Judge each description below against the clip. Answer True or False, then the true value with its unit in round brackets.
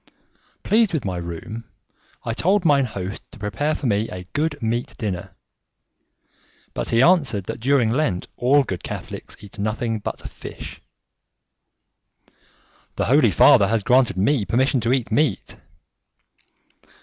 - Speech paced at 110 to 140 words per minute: True (135 wpm)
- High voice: False (115 Hz)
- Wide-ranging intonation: True (5.7 semitones)